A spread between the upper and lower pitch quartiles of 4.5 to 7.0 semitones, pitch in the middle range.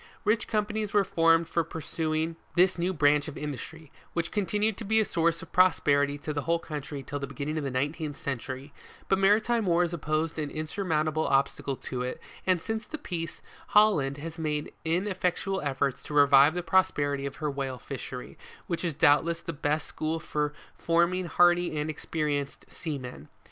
No: average, 3.6 semitones; medium, 160 Hz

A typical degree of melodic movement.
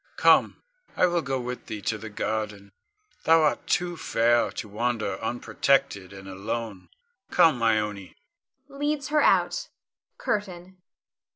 No: wide, 8.5 semitones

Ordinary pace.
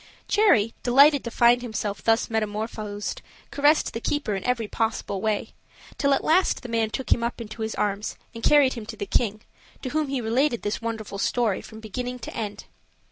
Yes: average, 190 wpm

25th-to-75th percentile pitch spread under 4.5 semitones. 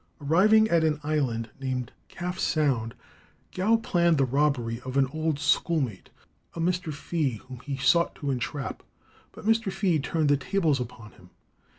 No: average, 4.8 semitones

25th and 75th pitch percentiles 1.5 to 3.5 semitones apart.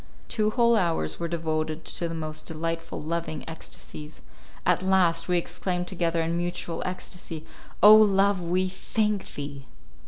Yes: narrow, 2.5 semitones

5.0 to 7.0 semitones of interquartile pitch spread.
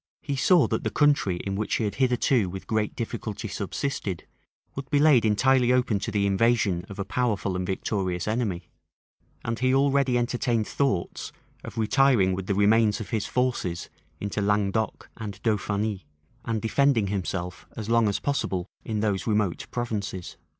No: average, 3.8 semitones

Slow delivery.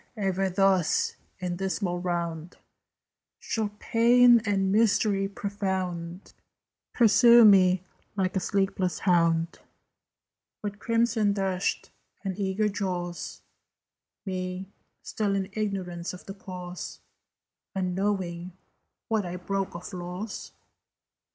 Yes: slow, 100 wpm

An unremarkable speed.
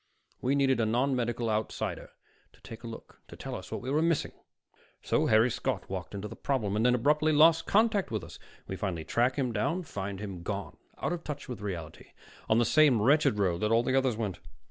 No: fast, 220 wpm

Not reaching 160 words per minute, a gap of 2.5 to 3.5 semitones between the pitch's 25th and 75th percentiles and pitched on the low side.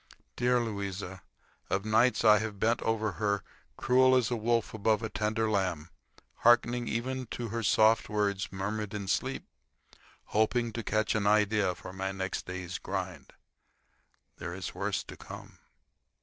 Yes: average, 150 wpm; average, 2.8 semitones; low, 110 Hz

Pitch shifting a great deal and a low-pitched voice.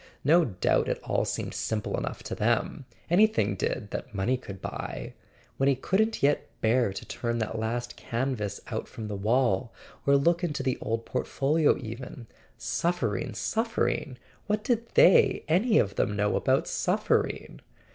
Yes: wide, 7.0 semitones; low, 125 Hz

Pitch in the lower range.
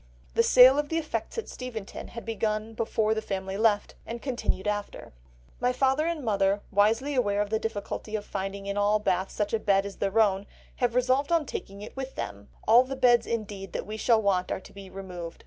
No: high, 215 Hz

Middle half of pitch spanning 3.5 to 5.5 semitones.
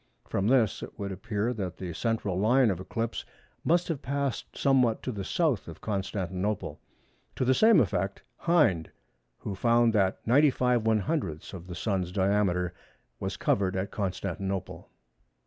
Yes: average, 4.7 semitones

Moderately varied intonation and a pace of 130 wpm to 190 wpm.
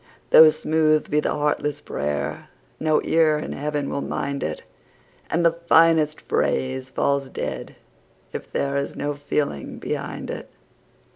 No: narrow, 1.9 semitones; average, 140 wpm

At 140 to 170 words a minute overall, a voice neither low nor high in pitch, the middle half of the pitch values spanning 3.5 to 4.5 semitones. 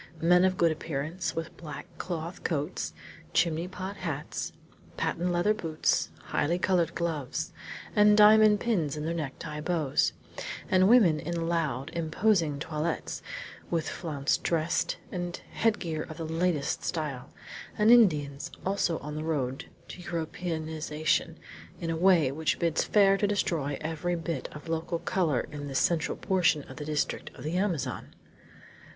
No: average, 145 wpm; medium, 165 Hz; average, 2.9 semitones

